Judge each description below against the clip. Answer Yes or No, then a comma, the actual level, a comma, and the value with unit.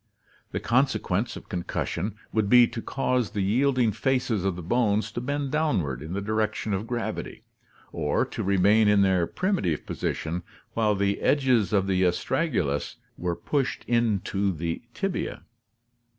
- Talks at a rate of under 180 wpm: Yes, average, 150 wpm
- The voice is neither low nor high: No, low, 105 Hz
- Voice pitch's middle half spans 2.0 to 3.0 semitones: No, average, 4.7 semitones